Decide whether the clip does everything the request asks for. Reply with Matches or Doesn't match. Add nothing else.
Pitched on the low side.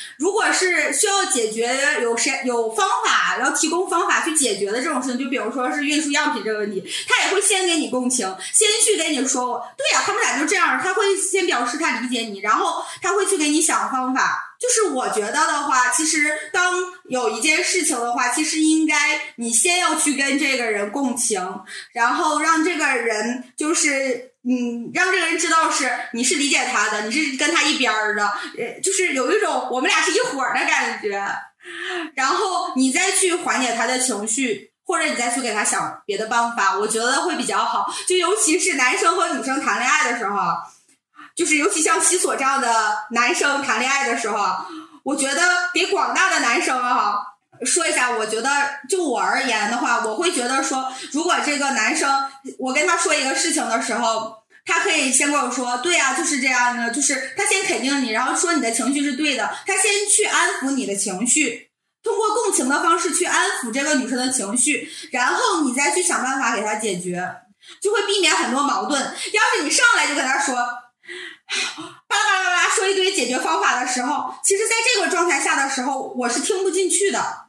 Doesn't match